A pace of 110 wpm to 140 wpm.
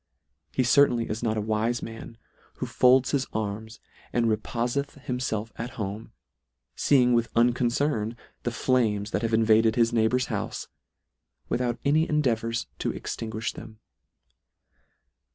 Yes: slow, 135 wpm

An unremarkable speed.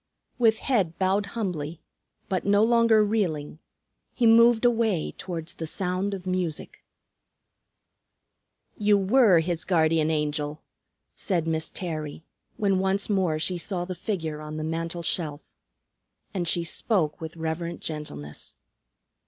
No: slow, 130 wpm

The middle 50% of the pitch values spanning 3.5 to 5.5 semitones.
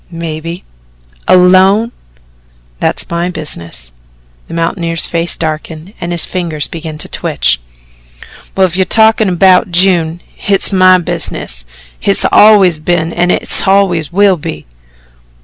No: narrow, 2.6 semitones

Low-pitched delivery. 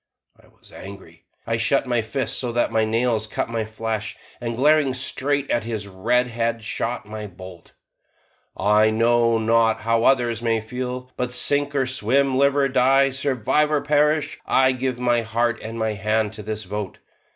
Yes: low, 115 Hz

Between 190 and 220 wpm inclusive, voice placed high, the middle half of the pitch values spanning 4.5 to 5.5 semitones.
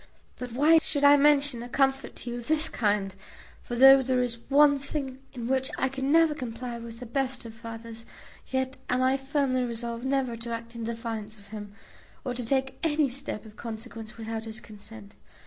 No: average, 200 wpm; high, 245 Hz; average, 2.9 semitones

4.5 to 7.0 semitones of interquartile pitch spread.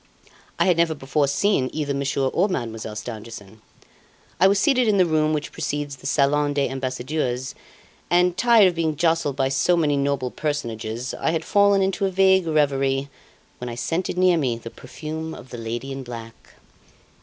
Yes: average, 5.0 semitones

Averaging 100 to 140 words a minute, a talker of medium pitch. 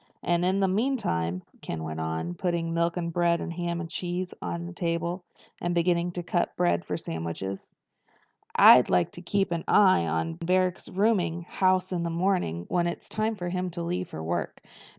No: average, 190 wpm; medium, 170 Hz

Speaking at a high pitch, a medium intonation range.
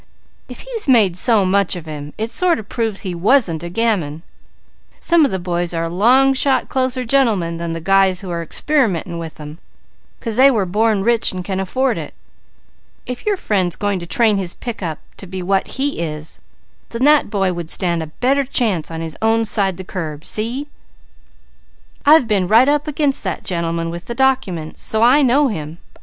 No: high, 200 Hz; wide, 6.5 semitones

